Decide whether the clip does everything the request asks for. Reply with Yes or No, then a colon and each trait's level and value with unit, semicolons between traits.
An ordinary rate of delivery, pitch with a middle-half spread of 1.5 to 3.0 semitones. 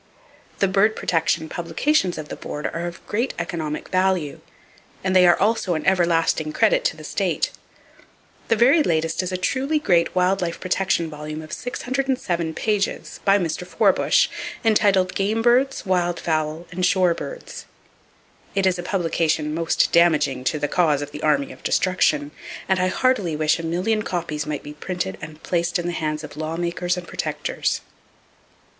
No: average, 165 wpm; average, 3.5 semitones